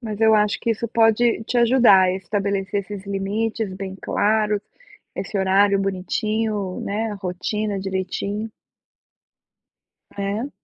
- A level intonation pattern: Yes, narrow, 2.2 semitones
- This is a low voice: No, high, 205 Hz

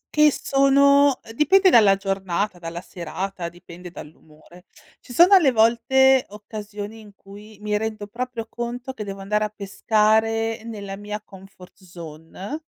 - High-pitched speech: Yes, high, 210 Hz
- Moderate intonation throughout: Yes, average, 3.5 semitones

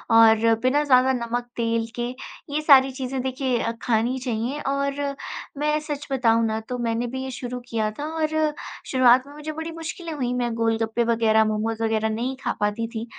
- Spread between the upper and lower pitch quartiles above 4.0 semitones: No, average, 3.3 semitones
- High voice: Yes, high, 245 Hz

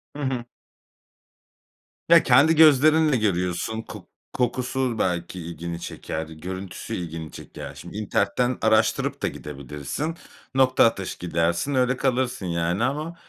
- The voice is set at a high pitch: No, low, 110 Hz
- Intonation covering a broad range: Yes, wide, 7.4 semitones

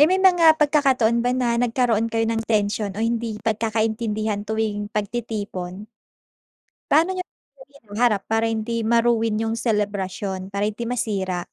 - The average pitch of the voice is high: Yes, high, 225 Hz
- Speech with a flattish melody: Yes, narrow, 2.3 semitones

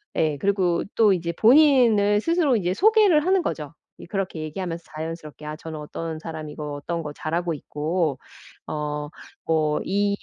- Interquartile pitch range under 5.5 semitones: Yes, average, 5.1 semitones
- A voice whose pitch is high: No, medium, 170 Hz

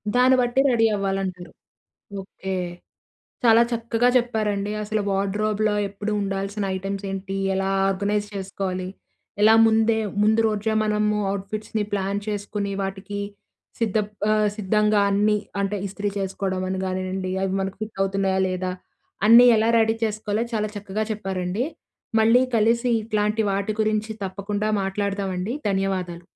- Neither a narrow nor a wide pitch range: No, narrow, 2.0 semitones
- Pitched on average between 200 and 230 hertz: Yes, high, 205 Hz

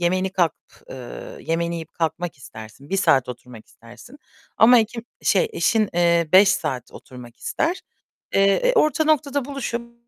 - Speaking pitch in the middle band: Yes, medium, 175 Hz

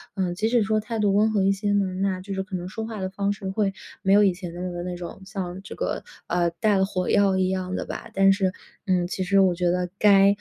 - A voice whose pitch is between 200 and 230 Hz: No, high, 190 Hz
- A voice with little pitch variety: Yes, narrow, 1.9 semitones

